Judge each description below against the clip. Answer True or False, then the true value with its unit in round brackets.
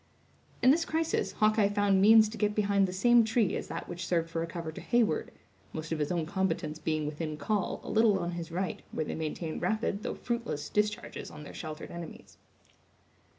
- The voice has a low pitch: False (190 Hz)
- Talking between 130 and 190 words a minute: False (200 wpm)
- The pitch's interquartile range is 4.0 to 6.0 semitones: True (4.8 semitones)